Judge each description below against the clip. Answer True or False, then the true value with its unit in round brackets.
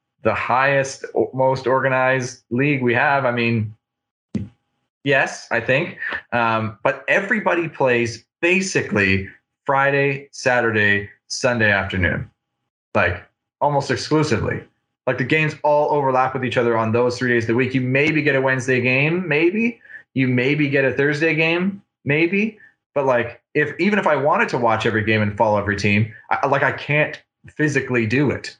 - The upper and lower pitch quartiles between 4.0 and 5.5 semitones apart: True (4.4 semitones)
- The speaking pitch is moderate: False (130 Hz)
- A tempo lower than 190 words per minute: True (155 wpm)